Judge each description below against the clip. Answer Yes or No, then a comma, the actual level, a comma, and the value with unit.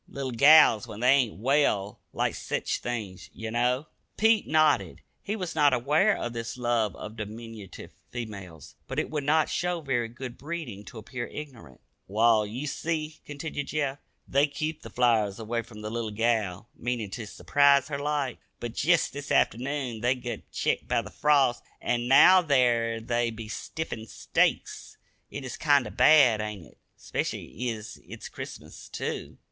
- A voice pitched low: Yes, low, 120 Hz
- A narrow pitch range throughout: No, average, 4.4 semitones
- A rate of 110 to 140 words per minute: No, average, 165 wpm